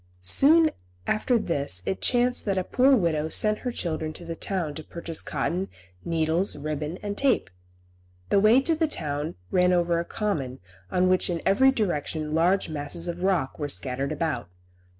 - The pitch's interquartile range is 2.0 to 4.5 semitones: No, average, 5.2 semitones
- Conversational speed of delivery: Yes, average, 170 wpm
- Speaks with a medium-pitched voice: Yes, medium, 170 Hz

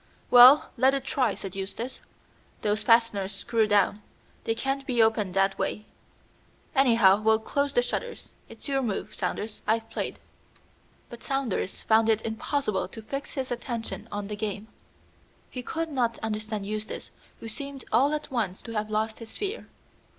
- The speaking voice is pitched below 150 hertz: No, high, 225 Hz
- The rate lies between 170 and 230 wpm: No, average, 160 wpm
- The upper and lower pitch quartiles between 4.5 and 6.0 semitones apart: No, average, 3.6 semitones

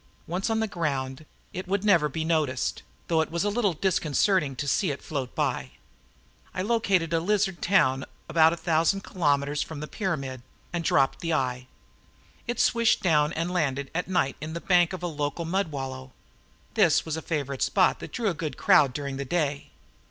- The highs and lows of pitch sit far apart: No, average, 4.6 semitones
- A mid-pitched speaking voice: Yes, medium, 160 Hz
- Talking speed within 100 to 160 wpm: No, average, 190 wpm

